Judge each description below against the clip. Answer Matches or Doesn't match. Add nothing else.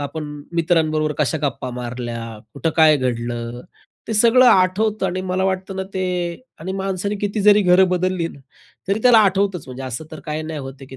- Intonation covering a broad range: Matches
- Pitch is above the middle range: Doesn't match